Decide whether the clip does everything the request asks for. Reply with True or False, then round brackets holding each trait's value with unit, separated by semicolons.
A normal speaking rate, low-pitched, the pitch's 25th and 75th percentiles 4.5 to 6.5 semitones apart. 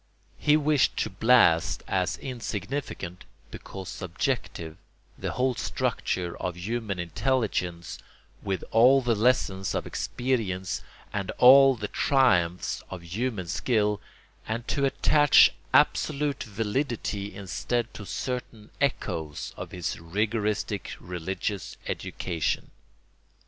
False (105 wpm; 105 Hz; 5.6 semitones)